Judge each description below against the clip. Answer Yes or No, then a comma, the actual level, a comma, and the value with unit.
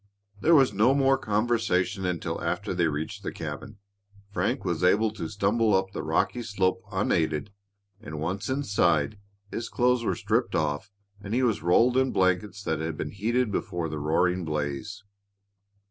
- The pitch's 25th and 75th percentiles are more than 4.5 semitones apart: Yes, average, 5.0 semitones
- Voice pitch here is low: Yes, low, 100 Hz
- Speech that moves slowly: No, average, 160 wpm